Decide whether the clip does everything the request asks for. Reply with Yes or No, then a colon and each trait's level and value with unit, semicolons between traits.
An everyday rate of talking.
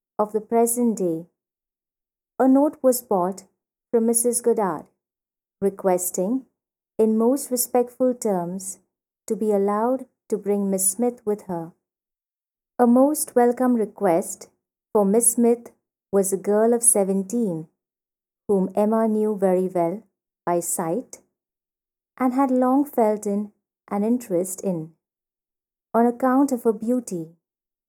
No: slow, 125 wpm